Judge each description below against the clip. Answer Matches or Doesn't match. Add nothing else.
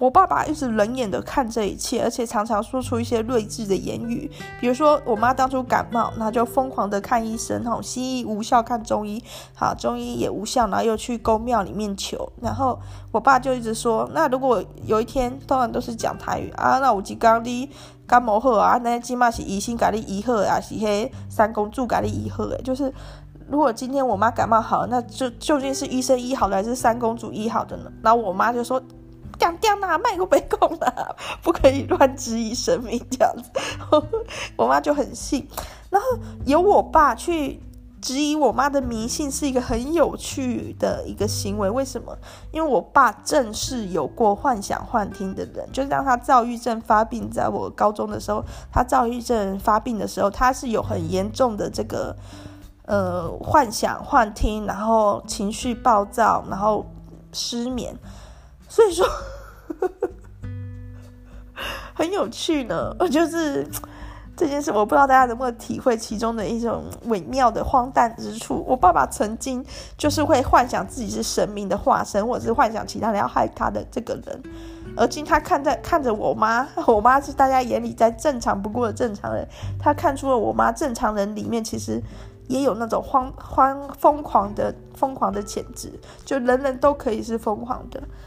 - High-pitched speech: Matches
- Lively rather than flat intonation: Doesn't match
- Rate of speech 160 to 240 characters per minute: Doesn't match